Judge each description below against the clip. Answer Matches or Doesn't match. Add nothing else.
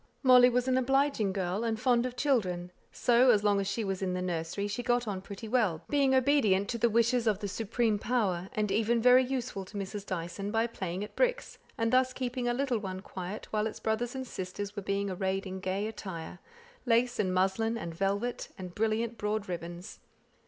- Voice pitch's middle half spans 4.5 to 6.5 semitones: Doesn't match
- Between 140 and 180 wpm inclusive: Doesn't match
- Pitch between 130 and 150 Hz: Doesn't match